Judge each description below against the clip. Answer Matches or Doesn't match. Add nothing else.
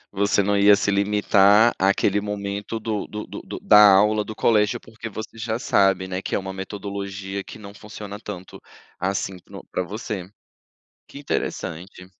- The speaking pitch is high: Doesn't match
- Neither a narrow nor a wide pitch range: Doesn't match